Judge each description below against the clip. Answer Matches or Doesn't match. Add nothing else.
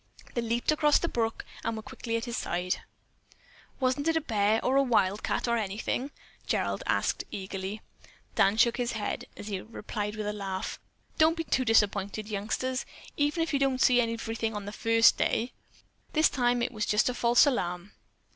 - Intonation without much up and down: Doesn't match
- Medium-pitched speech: Doesn't match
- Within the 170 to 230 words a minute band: Matches